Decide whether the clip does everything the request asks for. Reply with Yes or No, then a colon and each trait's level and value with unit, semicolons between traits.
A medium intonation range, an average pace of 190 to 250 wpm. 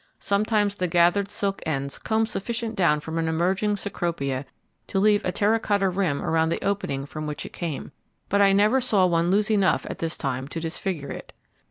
Yes: average, 4.0 semitones; average, 195 wpm